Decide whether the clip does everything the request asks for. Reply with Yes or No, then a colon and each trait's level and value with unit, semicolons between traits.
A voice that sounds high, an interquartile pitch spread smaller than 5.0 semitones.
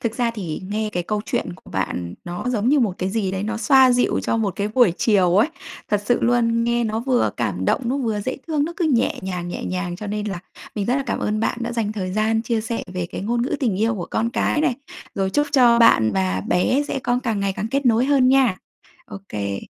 Yes: high, 220 Hz; average, 4.3 semitones